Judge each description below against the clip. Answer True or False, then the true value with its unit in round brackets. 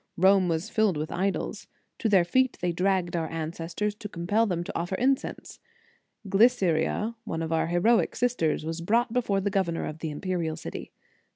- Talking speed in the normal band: True (180 wpm)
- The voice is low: False (185 Hz)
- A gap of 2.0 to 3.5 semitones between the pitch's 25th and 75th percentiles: False (4.2 semitones)